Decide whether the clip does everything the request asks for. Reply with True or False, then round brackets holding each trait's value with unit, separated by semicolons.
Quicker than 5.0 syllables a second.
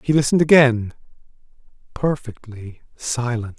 False (4.7 syllables/s)